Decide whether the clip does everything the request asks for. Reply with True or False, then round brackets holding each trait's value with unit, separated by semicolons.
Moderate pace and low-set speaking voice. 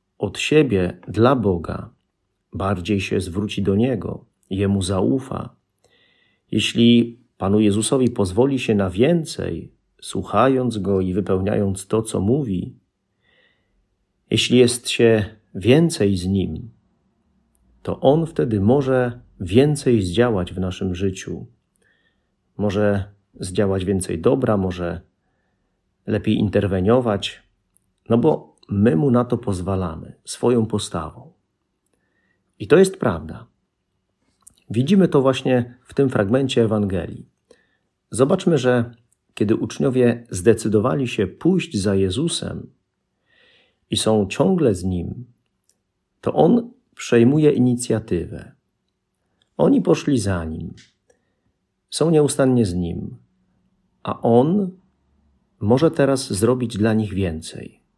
False (105 wpm; 110 Hz)